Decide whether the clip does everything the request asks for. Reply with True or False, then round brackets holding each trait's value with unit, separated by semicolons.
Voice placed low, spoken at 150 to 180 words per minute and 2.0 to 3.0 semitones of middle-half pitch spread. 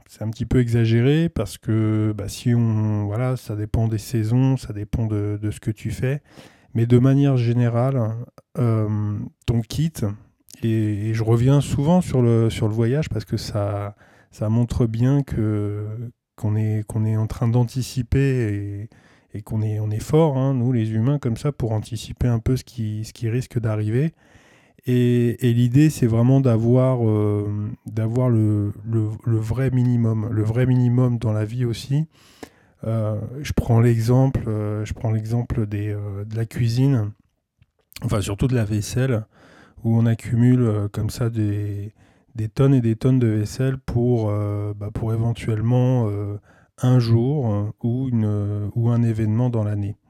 True (115 Hz; 165 wpm; 2.7 semitones)